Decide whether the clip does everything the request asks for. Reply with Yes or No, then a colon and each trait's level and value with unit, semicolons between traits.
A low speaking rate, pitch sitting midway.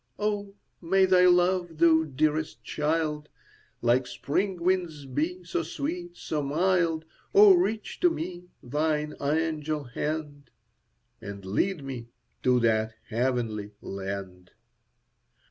Yes: slow, 110 wpm; medium, 155 Hz